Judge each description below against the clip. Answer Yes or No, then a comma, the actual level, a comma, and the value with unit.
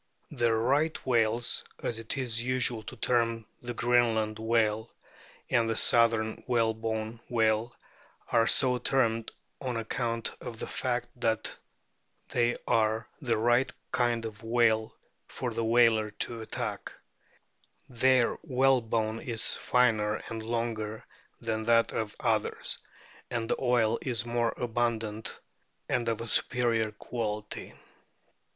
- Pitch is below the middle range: Yes, low, 115 Hz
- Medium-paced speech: No, slow, 130 wpm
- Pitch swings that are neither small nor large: No, narrow, 1.5 semitones